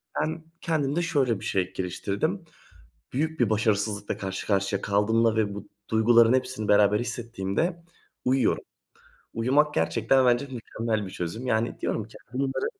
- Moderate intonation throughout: Yes, average, 4.5 semitones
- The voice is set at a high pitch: No, low, 115 Hz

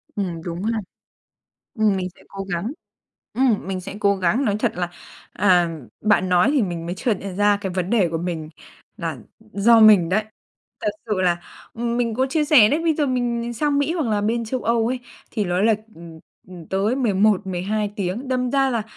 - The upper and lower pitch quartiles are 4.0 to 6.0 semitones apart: Yes, average, 4.5 semitones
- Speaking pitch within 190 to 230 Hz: Yes, high, 210 Hz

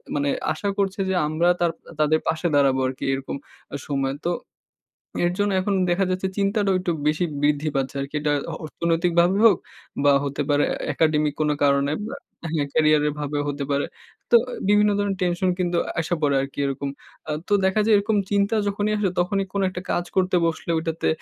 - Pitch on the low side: No, medium, 170 Hz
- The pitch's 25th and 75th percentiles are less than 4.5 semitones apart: No, average, 4.9 semitones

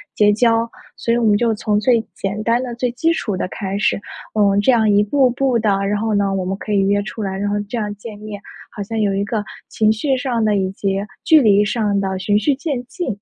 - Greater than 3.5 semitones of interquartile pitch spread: No, average, 2.7 semitones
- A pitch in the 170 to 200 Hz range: No, high, 215 Hz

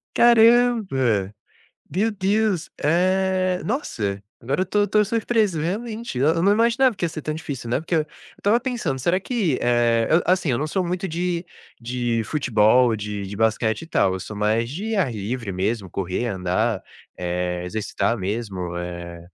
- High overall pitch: No, medium, 140 Hz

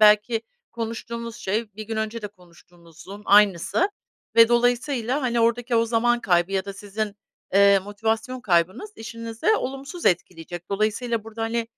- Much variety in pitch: No, average, 2.9 semitones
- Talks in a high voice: Yes, high, 225 Hz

